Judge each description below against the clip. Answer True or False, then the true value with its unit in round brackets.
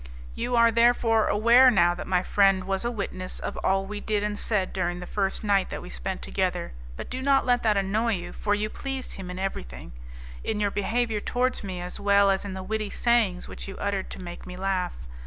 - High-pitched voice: True (200 Hz)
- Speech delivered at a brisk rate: True (225 wpm)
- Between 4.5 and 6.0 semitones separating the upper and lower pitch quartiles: False (3.3 semitones)